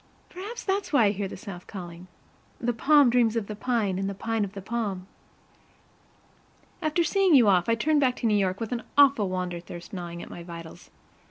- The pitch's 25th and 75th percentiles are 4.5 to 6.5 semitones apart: Yes, wide, 5.4 semitones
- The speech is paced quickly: Yes, fast, 210 wpm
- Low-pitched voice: No, high, 215 Hz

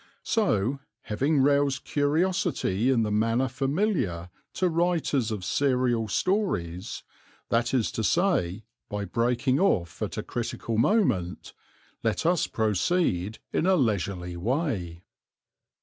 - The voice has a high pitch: No, low, 120 Hz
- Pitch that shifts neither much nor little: No, wide, 6.8 semitones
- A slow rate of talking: Yes, slow, 120 wpm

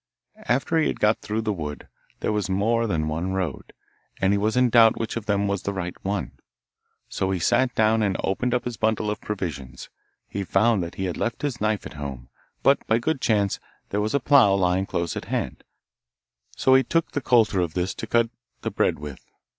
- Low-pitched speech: Yes, low, 105 Hz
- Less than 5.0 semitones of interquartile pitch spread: Yes, average, 3.8 semitones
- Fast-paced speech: Yes, fast, 210 wpm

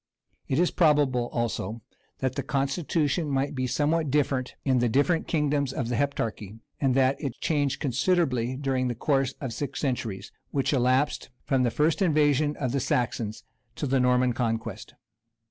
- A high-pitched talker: No, low, 135 Hz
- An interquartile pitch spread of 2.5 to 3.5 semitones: Yes, average, 2.9 semitones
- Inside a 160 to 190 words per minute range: Yes, average, 165 wpm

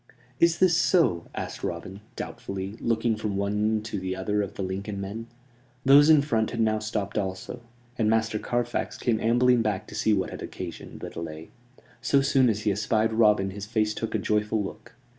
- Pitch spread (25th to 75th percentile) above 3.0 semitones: No, average, 2.7 semitones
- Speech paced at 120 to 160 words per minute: No, average, 190 wpm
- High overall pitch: No, low, 110 Hz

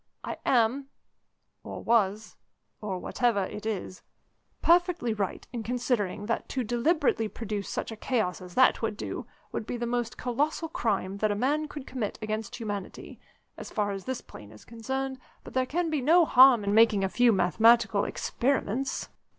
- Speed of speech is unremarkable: Yes, average, 170 wpm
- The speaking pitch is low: No, high, 230 Hz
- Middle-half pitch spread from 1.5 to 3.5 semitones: No, average, 4.0 semitones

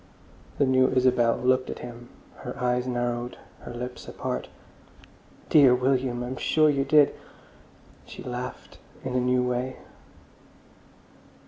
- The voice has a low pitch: Yes, low, 125 Hz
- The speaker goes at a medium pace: No, slow, 125 wpm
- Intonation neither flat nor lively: No, narrow, 1.0 semitones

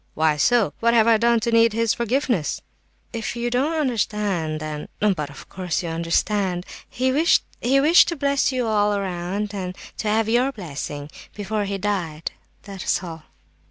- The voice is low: No, high, 210 Hz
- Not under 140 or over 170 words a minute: Yes, average, 160 wpm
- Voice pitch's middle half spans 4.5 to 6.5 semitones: Yes, average, 5.1 semitones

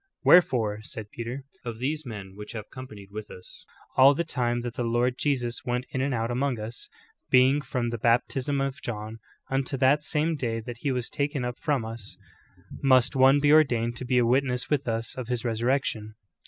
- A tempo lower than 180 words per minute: No, average, 200 wpm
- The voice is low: Yes, low, 125 Hz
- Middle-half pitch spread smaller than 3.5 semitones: Yes, average, 2.9 semitones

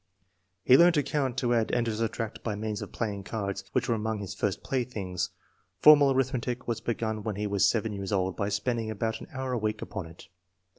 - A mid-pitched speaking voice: No, low, 110 Hz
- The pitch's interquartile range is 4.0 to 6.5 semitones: No, average, 3.3 semitones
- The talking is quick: Yes, fast, 215 wpm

